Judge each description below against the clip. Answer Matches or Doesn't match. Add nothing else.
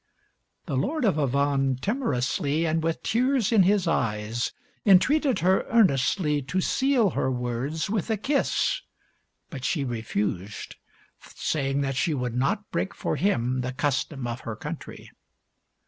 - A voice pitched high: Doesn't match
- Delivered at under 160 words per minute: Matches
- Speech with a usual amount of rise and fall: Doesn't match